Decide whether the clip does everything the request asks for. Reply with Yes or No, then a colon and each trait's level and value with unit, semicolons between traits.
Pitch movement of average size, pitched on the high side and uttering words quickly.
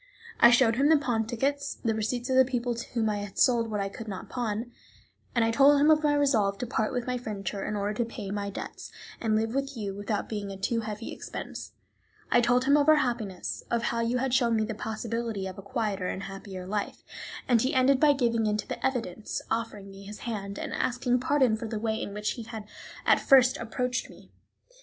Yes: average, 3.1 semitones; high, 230 Hz; fast, 230 wpm